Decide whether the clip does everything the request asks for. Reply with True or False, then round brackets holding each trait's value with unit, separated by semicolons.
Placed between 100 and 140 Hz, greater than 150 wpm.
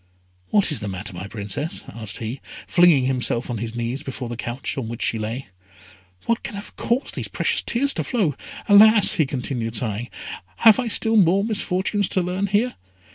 True (135 Hz; 185 wpm)